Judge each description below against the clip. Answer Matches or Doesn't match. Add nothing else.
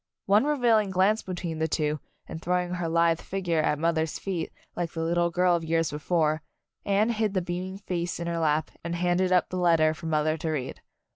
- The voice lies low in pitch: Doesn't match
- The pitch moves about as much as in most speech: Doesn't match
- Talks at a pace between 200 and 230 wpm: Matches